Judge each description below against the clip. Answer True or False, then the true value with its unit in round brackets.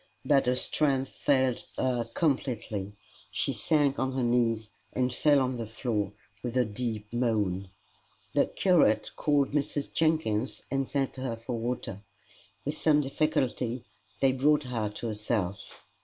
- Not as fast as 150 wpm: True (140 wpm)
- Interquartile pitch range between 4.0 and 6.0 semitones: False (3.6 semitones)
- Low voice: True (125 Hz)